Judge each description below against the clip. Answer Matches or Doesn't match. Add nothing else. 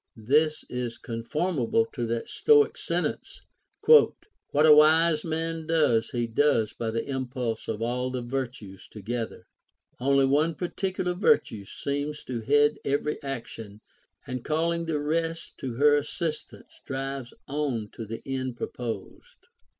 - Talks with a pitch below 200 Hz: Matches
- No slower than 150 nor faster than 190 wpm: Doesn't match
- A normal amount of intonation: Matches